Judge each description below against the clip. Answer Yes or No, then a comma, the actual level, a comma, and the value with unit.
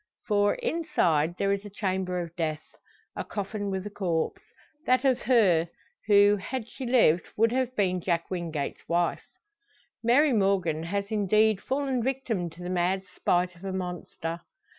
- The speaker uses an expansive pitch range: No, average, 4.3 semitones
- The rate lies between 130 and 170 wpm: Yes, average, 160 wpm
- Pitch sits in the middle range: No, high, 195 Hz